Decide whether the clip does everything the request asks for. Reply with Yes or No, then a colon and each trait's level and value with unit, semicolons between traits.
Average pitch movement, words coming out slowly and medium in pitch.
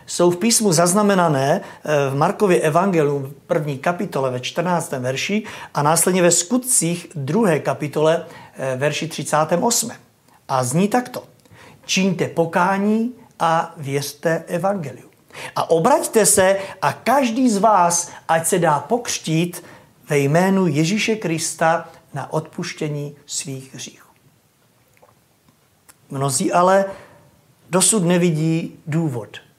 Yes: average, 4.6 semitones; slow, 105 wpm; medium, 165 Hz